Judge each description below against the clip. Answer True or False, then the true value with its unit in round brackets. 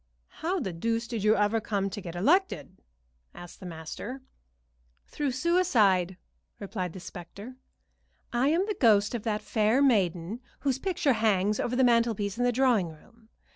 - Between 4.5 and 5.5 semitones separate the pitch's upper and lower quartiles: True (5.0 semitones)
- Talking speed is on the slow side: False (165 wpm)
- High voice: True (225 Hz)